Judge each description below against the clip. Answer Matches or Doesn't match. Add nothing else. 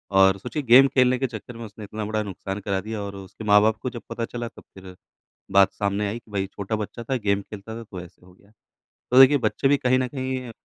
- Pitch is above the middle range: Doesn't match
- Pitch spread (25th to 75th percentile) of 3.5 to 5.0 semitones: Matches